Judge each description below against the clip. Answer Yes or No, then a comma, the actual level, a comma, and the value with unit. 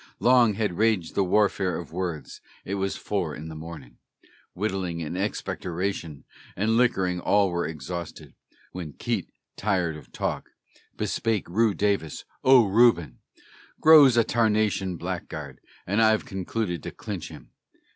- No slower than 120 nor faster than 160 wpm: Yes, slow, 135 wpm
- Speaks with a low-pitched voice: Yes, very low, 95 Hz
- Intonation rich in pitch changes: No, average, 4.2 semitones